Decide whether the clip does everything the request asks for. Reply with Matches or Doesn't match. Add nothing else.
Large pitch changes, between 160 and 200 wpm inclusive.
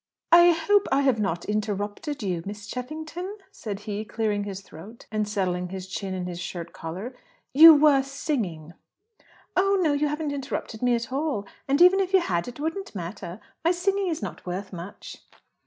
Matches